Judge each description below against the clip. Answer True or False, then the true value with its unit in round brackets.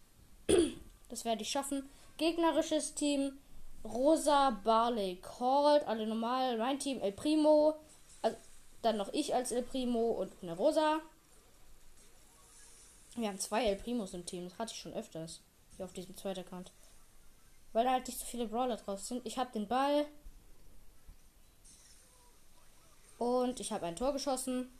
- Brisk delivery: False (150 wpm)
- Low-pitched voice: False (245 Hz)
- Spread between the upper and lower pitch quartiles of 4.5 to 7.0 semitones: True (4.8 semitones)